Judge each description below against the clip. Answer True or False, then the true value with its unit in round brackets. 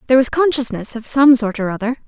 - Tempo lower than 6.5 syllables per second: False (6.6 syllables/s)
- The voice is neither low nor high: False (245 Hz)